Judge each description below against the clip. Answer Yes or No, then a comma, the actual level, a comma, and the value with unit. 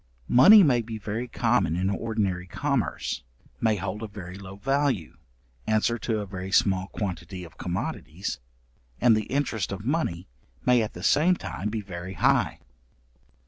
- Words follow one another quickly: No, average, 155 wpm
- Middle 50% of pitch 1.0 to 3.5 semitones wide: No, average, 4.3 semitones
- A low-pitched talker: Yes, low, 105 Hz